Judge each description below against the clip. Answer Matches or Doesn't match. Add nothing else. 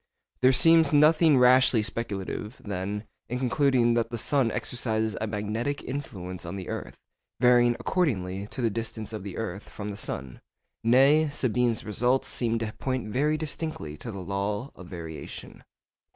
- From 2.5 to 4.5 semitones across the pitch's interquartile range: Matches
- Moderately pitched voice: Doesn't match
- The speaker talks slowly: Doesn't match